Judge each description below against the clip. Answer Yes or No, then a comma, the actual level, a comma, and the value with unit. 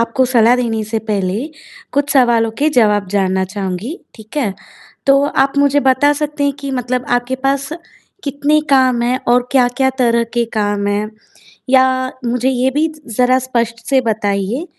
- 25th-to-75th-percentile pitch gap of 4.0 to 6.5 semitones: No, average, 3.6 semitones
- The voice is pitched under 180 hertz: No, high, 245 Hz